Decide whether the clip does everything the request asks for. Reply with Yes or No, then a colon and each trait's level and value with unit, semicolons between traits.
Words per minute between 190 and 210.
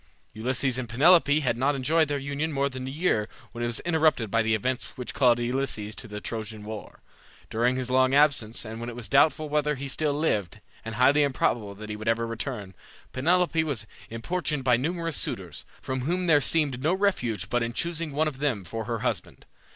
Yes: fast, 205 wpm